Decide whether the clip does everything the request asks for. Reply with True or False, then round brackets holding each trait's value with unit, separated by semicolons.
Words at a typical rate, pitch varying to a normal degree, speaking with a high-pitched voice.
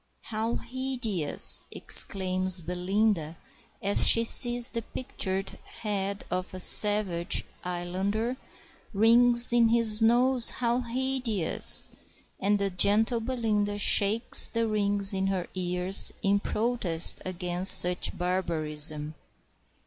False (105 wpm; 4.0 semitones; 205 Hz)